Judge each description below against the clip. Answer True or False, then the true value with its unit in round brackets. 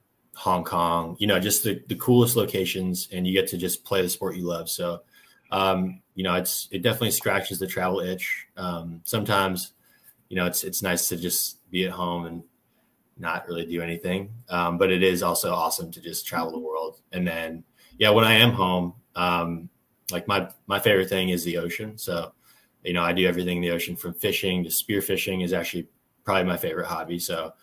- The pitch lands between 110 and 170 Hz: False (90 Hz)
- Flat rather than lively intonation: True (1.6 semitones)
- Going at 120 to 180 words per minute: False (205 wpm)